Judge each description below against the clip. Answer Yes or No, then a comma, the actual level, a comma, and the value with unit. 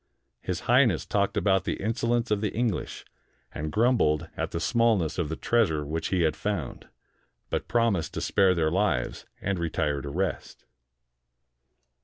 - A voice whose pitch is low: Yes, very low, 95 Hz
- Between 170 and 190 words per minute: No, average, 155 wpm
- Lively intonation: Yes, wide, 5.8 semitones